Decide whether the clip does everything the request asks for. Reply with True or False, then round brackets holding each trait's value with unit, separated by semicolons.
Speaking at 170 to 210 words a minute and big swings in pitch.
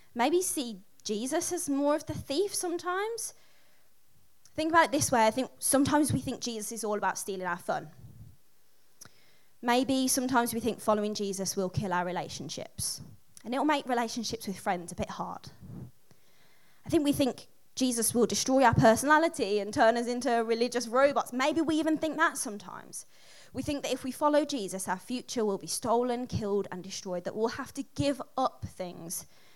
True (180 wpm; 5.7 semitones)